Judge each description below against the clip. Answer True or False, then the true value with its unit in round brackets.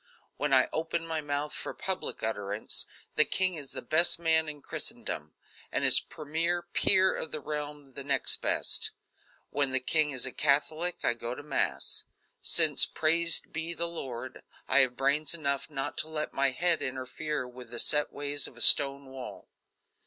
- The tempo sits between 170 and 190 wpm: True (175 wpm)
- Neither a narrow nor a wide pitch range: True (3.2 semitones)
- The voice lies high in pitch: False (145 Hz)